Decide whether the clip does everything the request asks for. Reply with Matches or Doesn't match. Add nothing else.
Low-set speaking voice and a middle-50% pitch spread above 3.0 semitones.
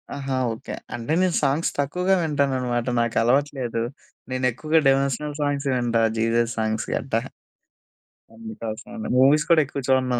Matches